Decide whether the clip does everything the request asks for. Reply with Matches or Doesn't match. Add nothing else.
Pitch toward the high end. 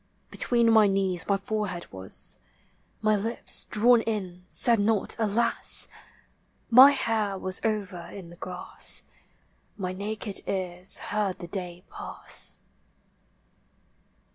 Matches